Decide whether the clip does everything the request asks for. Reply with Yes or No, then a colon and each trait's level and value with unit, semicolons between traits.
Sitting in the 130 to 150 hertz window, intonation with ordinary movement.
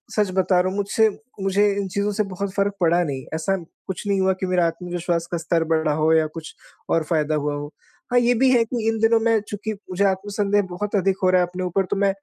No: high, 190 Hz; average, 3.1 semitones